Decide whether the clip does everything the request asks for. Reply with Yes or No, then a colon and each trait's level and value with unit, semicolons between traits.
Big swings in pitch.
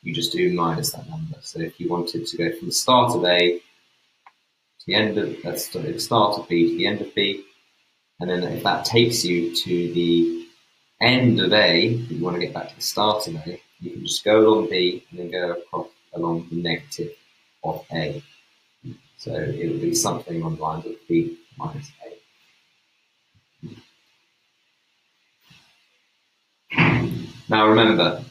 Yes: wide, 6.2 semitones